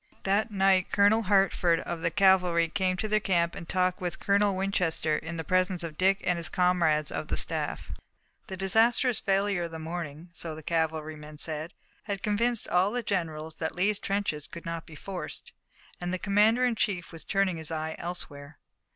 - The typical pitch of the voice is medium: Yes, medium, 180 Hz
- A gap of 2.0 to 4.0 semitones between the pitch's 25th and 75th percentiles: Yes, average, 3.3 semitones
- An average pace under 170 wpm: No, average, 185 wpm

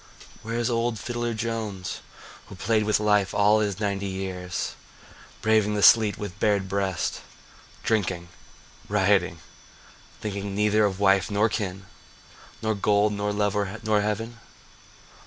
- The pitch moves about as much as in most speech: No, narrow, 1.9 semitones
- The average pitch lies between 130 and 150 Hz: No, low, 105 Hz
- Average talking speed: No, slow, 130 wpm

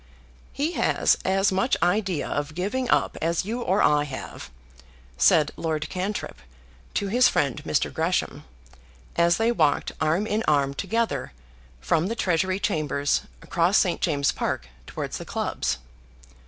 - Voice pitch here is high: No, medium, 175 Hz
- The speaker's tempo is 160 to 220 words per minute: No, average, 140 wpm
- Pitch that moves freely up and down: Yes, wide, 5.7 semitones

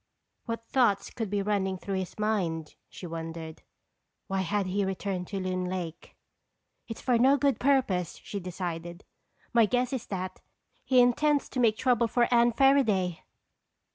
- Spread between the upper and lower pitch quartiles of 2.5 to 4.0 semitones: No, average, 4.8 semitones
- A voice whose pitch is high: Yes, high, 200 Hz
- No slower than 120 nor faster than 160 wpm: Yes, average, 155 wpm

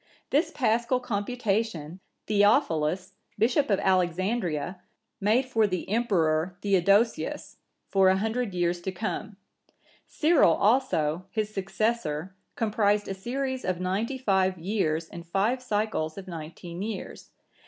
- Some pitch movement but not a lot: Yes, average, 4.1 semitones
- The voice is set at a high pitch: Yes, high, 200 Hz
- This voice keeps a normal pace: No, slow, 120 wpm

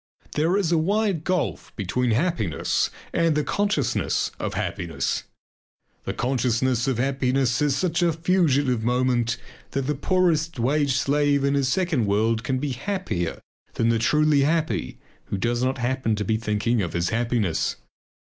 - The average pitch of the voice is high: No, low, 130 Hz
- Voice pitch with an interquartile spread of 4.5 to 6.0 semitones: Yes, average, 4.9 semitones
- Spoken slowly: No, average, 155 wpm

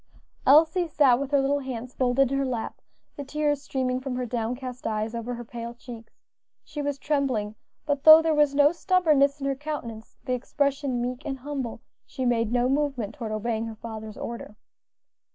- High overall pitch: Yes, very high, 260 Hz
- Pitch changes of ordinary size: Yes, average, 3.3 semitones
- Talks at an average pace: Yes, average, 185 wpm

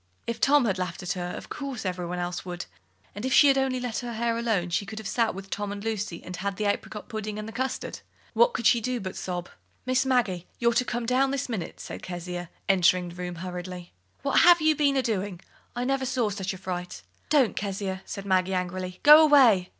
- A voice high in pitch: Yes, high, 205 Hz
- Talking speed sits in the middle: No, fast, 230 wpm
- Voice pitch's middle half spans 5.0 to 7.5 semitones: Yes, wide, 5.5 semitones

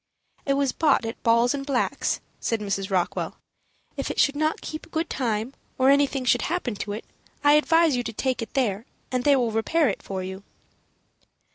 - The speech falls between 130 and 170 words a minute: No, average, 190 wpm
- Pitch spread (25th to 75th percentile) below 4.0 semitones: No, average, 4.4 semitones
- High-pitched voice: Yes, very high, 255 Hz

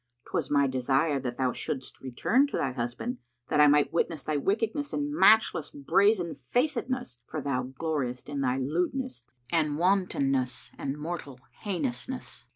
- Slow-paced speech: No, average, 145 wpm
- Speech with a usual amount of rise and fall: No, wide, 7.7 semitones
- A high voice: No, medium, 150 Hz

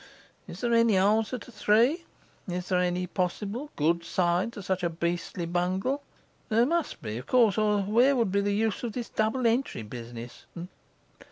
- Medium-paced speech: Yes, average, 180 wpm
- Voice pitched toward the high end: Yes, high, 200 Hz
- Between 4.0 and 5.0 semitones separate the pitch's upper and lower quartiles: Yes, average, 4.7 semitones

